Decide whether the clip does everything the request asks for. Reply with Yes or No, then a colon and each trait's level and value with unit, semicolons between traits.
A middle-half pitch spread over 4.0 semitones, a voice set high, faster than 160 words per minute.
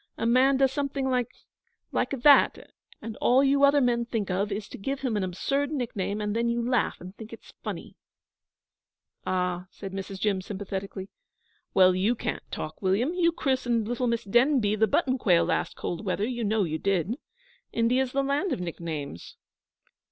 Yes: average, 5.2 semitones; high, 225 Hz; average, 175 wpm